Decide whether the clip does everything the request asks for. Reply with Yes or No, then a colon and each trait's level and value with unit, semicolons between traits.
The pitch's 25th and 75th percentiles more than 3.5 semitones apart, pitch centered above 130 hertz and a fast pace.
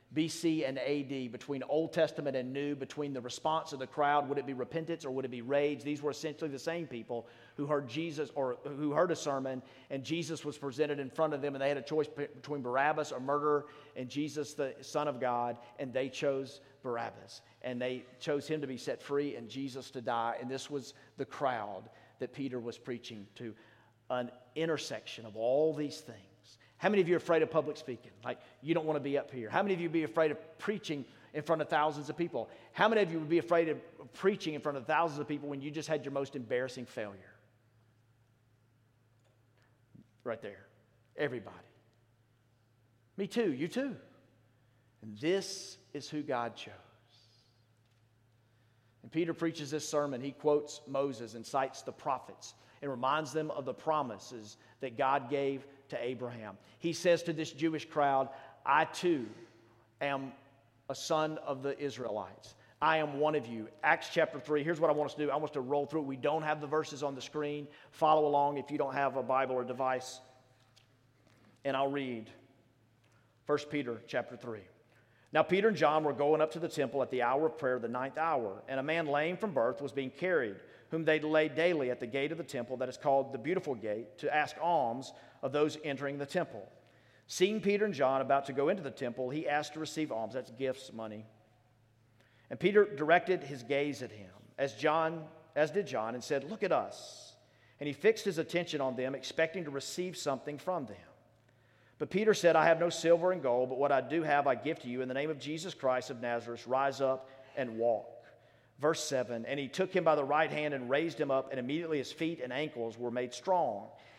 Yes: average, 4.2 semitones; medium, 140 Hz; fast, 210 wpm